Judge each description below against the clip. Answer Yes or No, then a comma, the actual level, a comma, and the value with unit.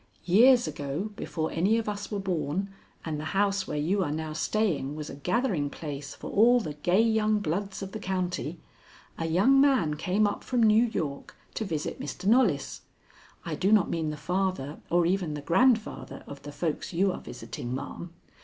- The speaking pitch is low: No, medium, 180 Hz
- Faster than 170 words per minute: Yes, average, 190 wpm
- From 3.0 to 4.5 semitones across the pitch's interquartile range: No, wide, 5.6 semitones